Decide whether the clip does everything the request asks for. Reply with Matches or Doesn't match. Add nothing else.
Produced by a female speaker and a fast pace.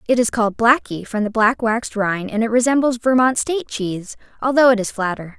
Matches